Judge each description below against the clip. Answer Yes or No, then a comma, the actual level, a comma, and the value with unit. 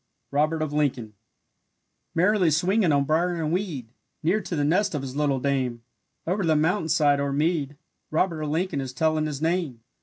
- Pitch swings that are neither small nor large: Yes, average, 3.4 semitones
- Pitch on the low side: No, medium, 155 Hz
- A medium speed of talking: Yes, average, 175 wpm